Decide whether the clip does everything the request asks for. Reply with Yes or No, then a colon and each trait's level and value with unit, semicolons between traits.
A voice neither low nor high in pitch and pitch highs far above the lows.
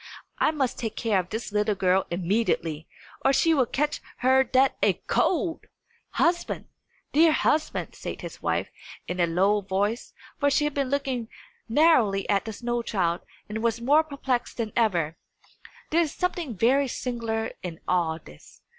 No: high, 230 Hz; wide, 6.1 semitones